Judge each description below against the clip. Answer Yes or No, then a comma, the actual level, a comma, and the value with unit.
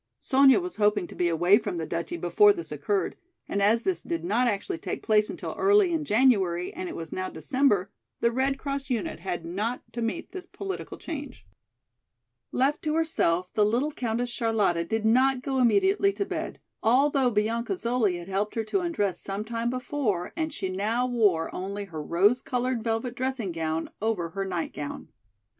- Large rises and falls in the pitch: Yes, wide, 5.8 semitones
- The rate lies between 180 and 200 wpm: Yes, average, 190 wpm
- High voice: Yes, high, 225 Hz